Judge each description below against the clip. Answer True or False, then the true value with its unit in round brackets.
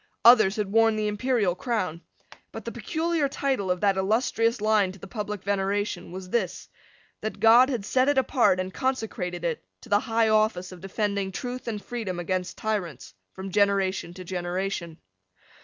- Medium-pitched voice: False (205 Hz)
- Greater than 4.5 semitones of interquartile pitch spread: False (3.5 semitones)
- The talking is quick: False (170 wpm)